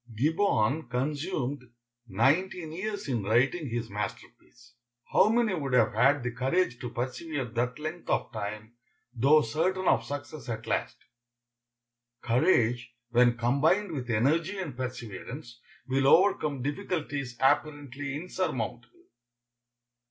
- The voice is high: No, low, 135 Hz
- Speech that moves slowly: Yes, slow, 115 wpm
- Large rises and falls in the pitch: No, average, 4.8 semitones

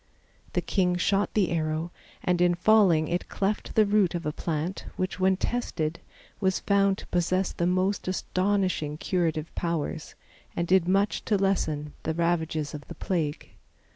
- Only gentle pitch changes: No, average, 3.1 semitones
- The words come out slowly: No, average, 160 wpm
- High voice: No, medium, 180 Hz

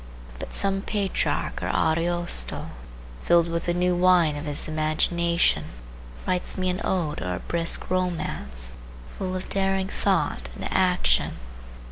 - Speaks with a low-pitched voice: No, medium, 170 Hz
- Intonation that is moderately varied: Yes, average, 3.0 semitones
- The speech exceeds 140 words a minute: No, slow, 135 wpm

